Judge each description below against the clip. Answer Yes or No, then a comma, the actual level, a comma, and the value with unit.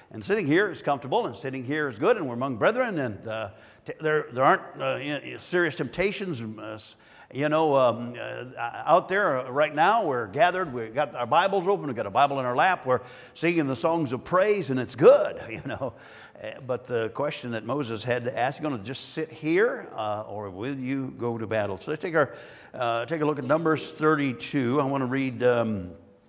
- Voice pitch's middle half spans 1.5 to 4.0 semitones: No, average, 4.6 semitones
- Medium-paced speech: No, fast, 215 wpm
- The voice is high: No, low, 135 Hz